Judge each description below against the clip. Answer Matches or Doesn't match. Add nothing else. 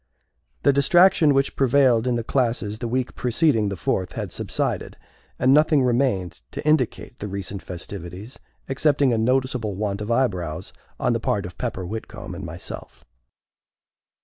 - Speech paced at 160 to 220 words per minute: Doesn't match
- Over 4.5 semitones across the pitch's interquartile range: Matches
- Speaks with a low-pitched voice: Matches